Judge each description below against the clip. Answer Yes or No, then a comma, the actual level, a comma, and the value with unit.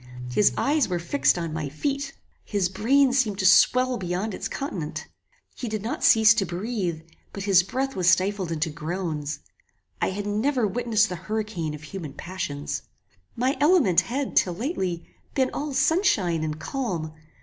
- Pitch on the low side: No, high, 195 Hz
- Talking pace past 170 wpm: No, average, 160 wpm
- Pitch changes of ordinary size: No, wide, 6.5 semitones